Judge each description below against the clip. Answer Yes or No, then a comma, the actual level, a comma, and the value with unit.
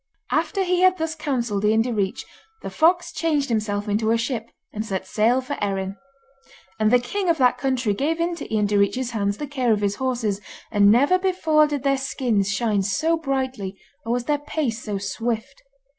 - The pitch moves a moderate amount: No, wide, 5.9 semitones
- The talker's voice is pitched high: Yes, high, 245 Hz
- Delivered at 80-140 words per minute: No, average, 190 wpm